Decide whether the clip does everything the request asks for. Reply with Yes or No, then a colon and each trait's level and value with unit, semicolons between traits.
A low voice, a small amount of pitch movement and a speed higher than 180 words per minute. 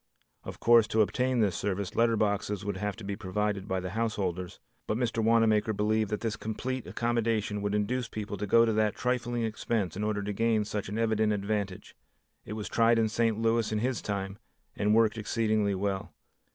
Yes: low, 110 Hz; narrow, 1.9 semitones; average, 195 wpm